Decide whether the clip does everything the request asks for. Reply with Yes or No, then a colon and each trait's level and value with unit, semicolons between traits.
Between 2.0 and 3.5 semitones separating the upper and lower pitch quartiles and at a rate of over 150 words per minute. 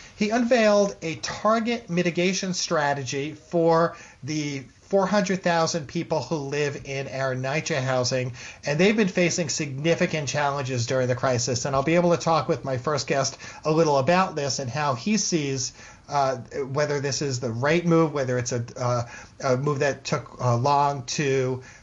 No: average, 4.2 semitones; average, 170 wpm